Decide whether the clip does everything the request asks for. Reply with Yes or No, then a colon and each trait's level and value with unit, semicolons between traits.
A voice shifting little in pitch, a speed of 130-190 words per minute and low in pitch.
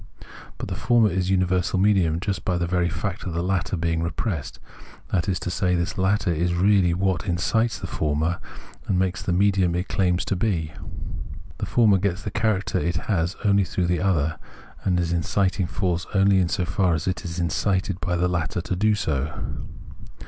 No: narrow, 2.2 semitones; average, 200 wpm; very low, 90 Hz